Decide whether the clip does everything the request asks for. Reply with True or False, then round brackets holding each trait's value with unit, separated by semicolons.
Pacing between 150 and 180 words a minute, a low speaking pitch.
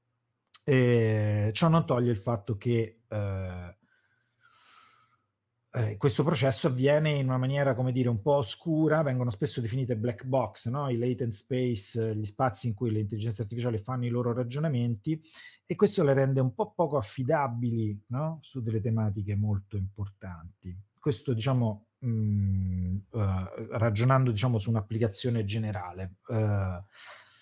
False (140 wpm; 120 Hz)